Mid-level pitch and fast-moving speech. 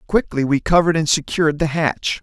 No: medium, 160 Hz; average, 190 wpm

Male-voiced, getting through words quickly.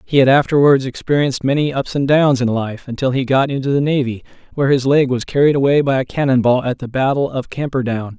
Yes: male; fast, 225 wpm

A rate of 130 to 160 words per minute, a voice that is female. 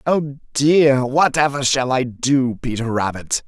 No: average, 140 wpm; male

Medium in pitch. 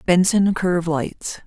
Yes: medium, 175 Hz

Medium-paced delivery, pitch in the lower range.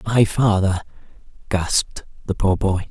No: slow, 125 wpm; low, 100 Hz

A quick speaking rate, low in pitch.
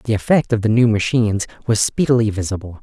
No: average, 190 wpm; low, 110 Hz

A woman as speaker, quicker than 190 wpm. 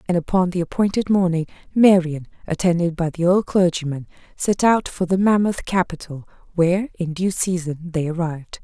No: female; average, 160 wpm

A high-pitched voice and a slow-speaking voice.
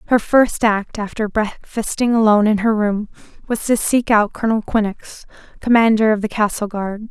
No: high, 215 Hz; average, 170 wpm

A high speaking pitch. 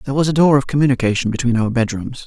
No: low, 130 Hz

